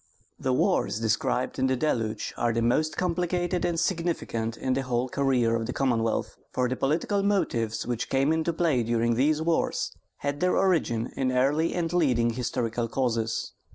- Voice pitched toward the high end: No, low, 130 Hz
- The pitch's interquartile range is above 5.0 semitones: Yes, wide, 5.6 semitones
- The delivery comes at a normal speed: Yes, average, 170 wpm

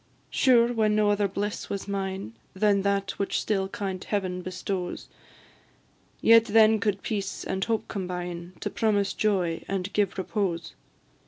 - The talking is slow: No, average, 145 wpm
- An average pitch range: No, narrow, 2.2 semitones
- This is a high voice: Yes, high, 200 Hz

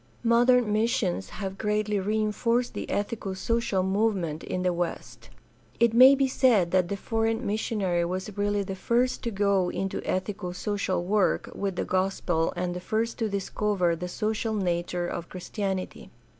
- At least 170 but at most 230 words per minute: No, average, 160 wpm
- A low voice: No, high, 200 Hz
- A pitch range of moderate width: Yes, average, 3.4 semitones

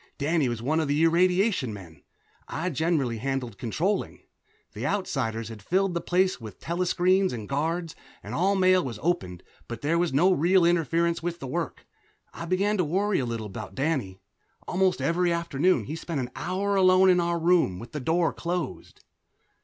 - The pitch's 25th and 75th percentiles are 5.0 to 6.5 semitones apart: Yes, wide, 5.4 semitones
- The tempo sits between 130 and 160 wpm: No, average, 175 wpm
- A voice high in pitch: No, medium, 165 Hz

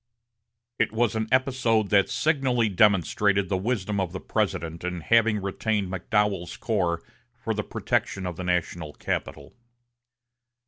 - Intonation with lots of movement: No, average, 3.7 semitones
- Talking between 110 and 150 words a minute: Yes, slow, 135 wpm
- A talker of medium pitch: No, low, 100 Hz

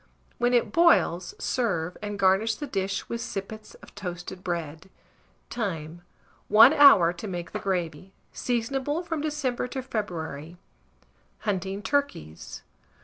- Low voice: No, high, 200 Hz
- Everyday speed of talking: No, slow, 125 wpm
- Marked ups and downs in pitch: Yes, wide, 6.1 semitones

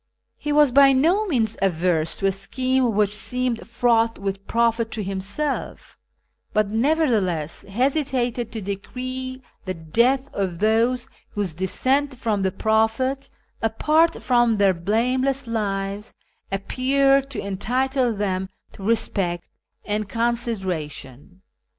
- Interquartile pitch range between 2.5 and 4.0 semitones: No, average, 4.8 semitones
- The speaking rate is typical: No, slow, 120 wpm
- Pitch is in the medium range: No, high, 225 Hz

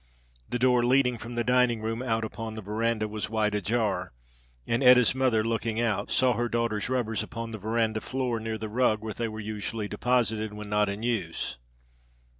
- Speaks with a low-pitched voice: Yes, low, 115 Hz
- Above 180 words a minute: Yes, average, 190 wpm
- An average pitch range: No, narrow, 1.9 semitones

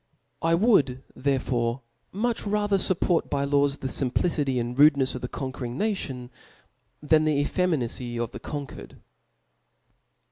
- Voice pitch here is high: No, medium, 140 Hz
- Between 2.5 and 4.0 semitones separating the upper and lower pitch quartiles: No, average, 4.6 semitones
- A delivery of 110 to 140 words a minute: Yes, slow, 135 wpm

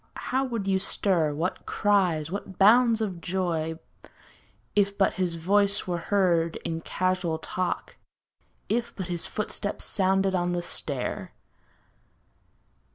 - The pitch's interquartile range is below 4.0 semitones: Yes, average, 2.9 semitones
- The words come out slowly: Yes, slow, 125 wpm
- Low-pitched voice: No, medium, 185 Hz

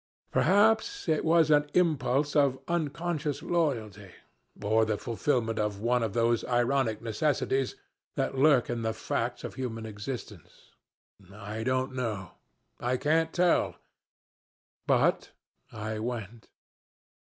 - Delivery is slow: Yes, slow, 120 wpm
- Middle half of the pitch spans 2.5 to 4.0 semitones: No, average, 5.1 semitones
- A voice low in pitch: Yes, low, 125 Hz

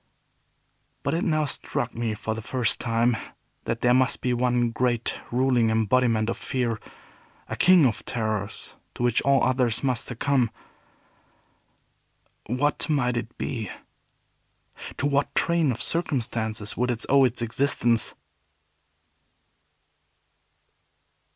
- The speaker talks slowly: Yes, slow, 125 wpm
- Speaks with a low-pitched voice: Yes, low, 120 Hz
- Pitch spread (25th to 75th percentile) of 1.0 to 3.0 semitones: Yes, narrow, 2.6 semitones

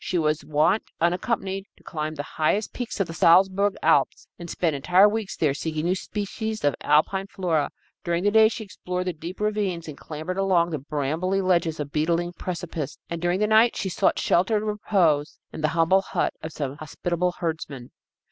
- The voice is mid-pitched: Yes, medium, 175 Hz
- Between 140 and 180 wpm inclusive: No, average, 190 wpm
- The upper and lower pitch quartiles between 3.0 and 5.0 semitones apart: Yes, average, 3.8 semitones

